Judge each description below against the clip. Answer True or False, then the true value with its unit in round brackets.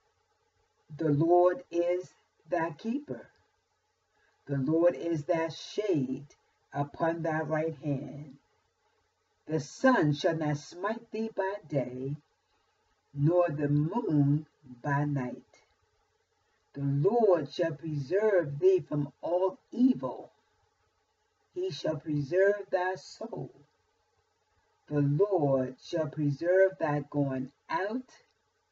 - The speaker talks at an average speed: False (100 wpm)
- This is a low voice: False (165 Hz)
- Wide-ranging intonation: True (5.8 semitones)